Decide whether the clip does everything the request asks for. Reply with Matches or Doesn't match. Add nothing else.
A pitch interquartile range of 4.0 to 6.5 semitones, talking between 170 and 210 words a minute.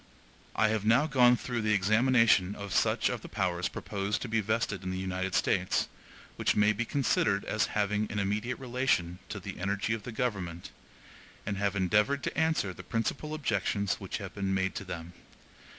Doesn't match